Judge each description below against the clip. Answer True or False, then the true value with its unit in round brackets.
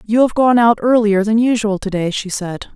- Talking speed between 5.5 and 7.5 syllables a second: False (4.9 syllables/s)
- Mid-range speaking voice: False (215 Hz)